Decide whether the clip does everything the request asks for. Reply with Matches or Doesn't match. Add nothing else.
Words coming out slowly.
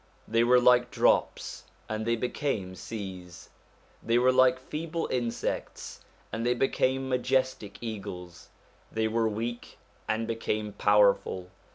Matches